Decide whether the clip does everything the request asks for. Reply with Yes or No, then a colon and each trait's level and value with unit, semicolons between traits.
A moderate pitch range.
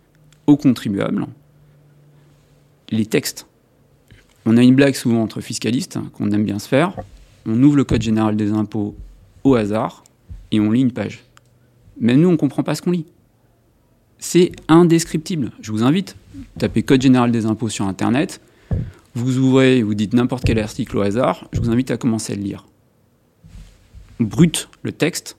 Yes: average, 4.7 semitones